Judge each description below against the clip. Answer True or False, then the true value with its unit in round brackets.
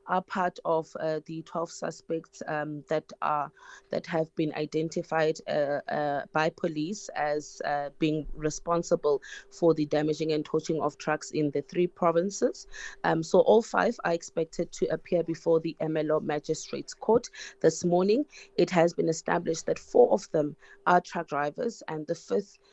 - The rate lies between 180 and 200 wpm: False (165 wpm)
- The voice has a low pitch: False (160 Hz)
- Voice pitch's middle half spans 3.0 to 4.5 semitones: False (2.5 semitones)